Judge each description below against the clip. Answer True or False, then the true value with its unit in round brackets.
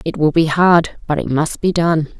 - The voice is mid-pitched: True (160 Hz)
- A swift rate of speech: True (245 wpm)